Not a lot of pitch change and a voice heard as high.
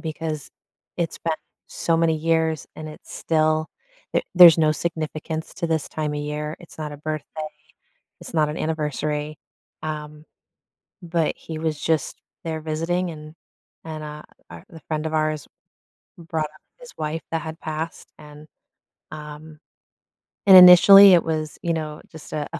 No: narrow, 1.2 semitones; medium, 155 Hz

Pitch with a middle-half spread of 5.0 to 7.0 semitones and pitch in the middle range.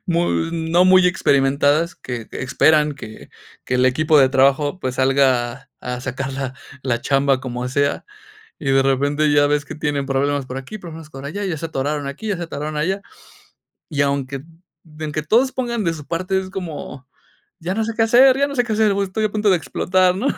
Yes: average, 5.3 semitones; medium, 150 Hz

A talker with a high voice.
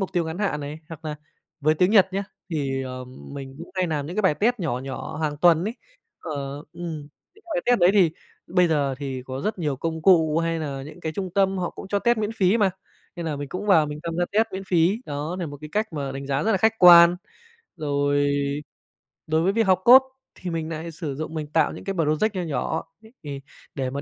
No: medium, 165 Hz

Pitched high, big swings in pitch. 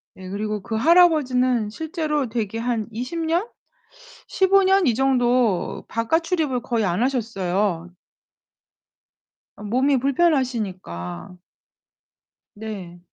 Yes: high, 240 Hz; wide, 6.0 semitones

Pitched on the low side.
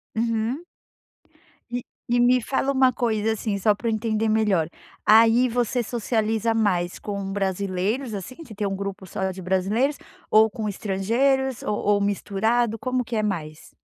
No: high, 220 Hz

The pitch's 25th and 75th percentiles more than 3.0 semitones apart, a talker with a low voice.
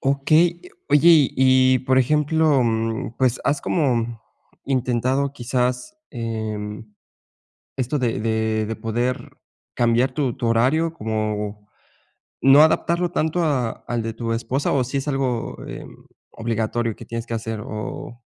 Yes: average, 3.5 semitones; low, 125 Hz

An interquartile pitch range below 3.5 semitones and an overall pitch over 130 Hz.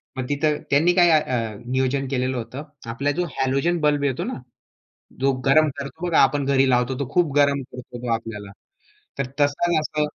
Yes: average, 2.8 semitones; medium, 140 Hz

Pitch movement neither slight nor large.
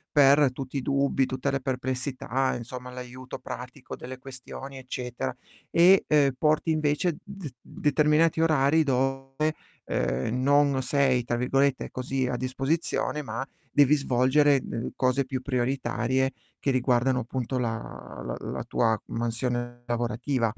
No: narrow, 2.0 semitones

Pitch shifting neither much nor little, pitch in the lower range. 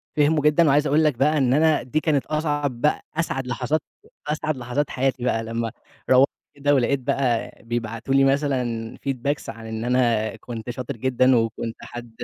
Yes: average, 3.6 semitones; low, 130 Hz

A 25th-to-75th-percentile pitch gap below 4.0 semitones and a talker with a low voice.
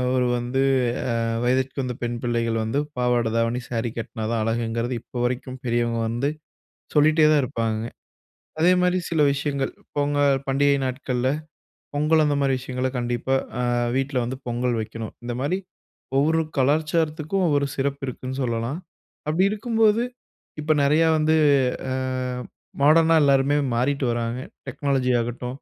Yes: average, 3.4 semitones; low, 130 Hz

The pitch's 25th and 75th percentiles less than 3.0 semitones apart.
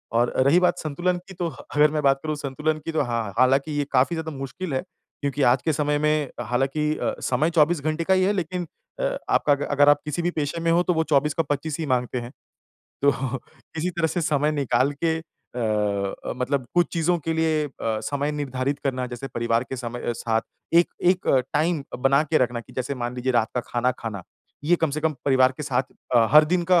No: average, 3.8 semitones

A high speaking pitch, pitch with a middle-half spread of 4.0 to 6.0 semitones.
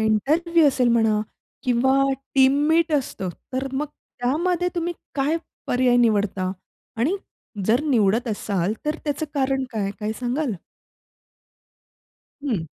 Yes: very high, 255 Hz; wide, 5.4 semitones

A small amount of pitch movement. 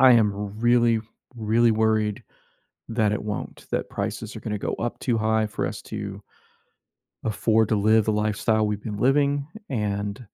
Yes: narrow, 1.8 semitones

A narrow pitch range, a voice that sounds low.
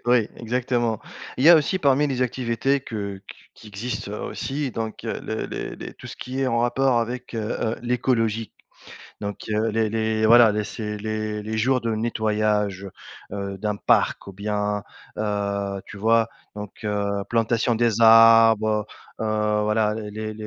Yes: narrow, 2.1 semitones; low, 110 Hz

